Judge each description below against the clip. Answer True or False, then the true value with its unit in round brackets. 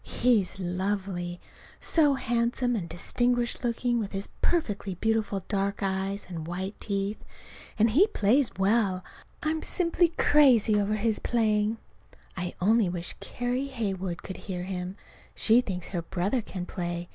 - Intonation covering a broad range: False (4.2 semitones)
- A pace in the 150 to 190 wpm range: False (140 wpm)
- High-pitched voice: True (205 Hz)